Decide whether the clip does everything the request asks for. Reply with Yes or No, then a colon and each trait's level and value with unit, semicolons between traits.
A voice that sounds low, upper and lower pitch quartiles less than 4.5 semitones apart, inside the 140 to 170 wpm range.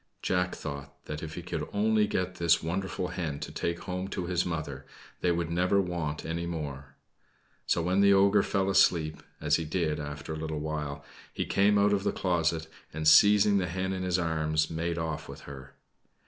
No: very low, 85 Hz; average, 3.1 semitones; average, 195 wpm